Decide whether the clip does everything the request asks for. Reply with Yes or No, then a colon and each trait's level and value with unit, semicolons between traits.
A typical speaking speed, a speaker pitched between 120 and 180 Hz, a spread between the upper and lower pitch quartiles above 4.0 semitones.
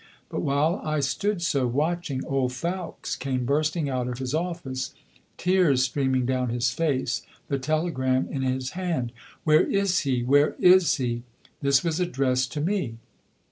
Yes: average, 155 wpm; medium, 140 Hz; average, 4.5 semitones